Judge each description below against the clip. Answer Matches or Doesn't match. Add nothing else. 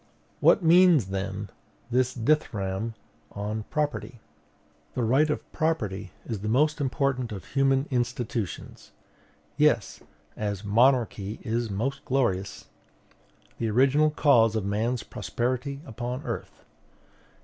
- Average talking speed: Doesn't match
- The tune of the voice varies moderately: Matches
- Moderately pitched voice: Doesn't match